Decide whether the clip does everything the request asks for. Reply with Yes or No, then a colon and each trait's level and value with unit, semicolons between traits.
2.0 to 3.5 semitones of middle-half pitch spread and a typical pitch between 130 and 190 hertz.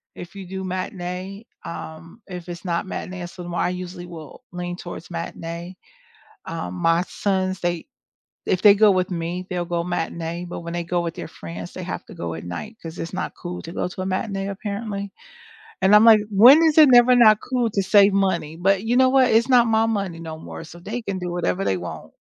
Yes: average, 3.0 semitones; medium, 185 Hz